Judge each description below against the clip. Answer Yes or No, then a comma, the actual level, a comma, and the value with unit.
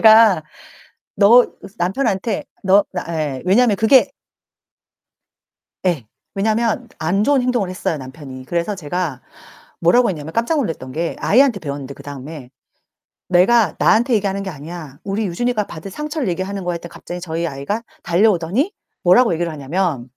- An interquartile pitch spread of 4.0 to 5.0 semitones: No, wide, 5.5 semitones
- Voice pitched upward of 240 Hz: No, medium, 185 Hz